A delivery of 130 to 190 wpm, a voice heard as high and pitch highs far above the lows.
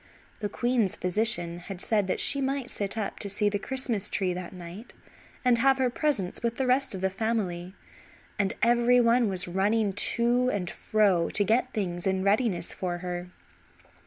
No: average, 180 wpm; high, 205 Hz; average, 4.5 semitones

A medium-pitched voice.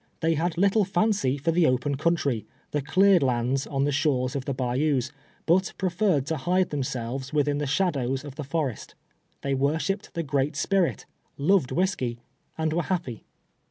Yes: medium, 145 Hz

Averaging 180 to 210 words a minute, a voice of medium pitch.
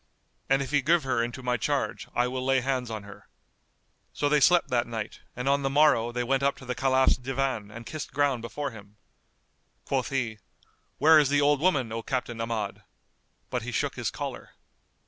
No: average, 200 wpm; low, 130 Hz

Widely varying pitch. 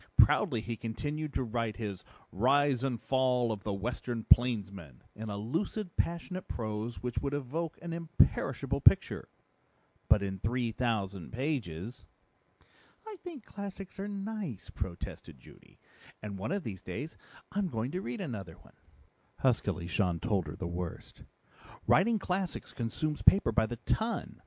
Yes: wide, 8.0 semitones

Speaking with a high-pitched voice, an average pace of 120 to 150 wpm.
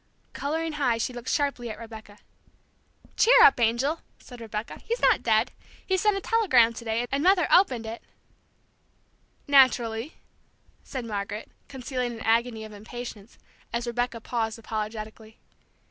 Yes: high, 235 Hz; average, 145 wpm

